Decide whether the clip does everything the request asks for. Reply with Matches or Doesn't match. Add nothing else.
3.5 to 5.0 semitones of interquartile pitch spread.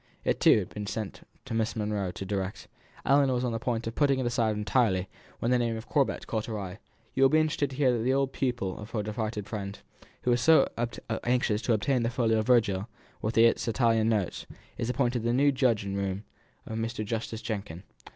Doesn't match